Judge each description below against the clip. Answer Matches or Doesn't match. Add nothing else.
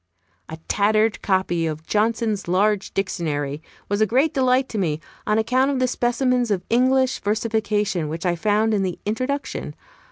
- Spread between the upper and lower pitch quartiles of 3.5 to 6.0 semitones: Matches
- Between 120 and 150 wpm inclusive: Doesn't match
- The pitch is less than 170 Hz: Doesn't match